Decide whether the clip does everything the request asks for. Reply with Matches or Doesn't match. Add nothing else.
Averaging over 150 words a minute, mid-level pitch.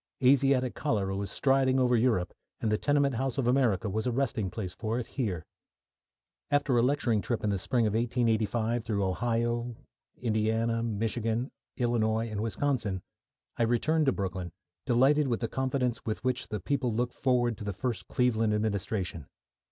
Doesn't match